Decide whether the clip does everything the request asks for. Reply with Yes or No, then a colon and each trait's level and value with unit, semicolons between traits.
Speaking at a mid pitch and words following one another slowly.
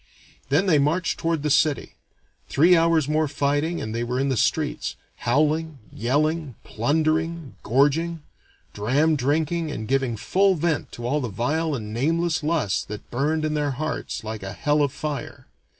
No: medium, 150 Hz; average, 165 wpm